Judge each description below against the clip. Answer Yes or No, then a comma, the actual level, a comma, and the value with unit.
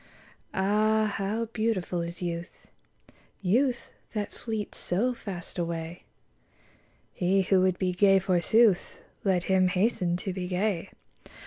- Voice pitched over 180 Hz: Yes, high, 190 Hz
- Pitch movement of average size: Yes, average, 3.2 semitones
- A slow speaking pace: Yes, slow, 125 wpm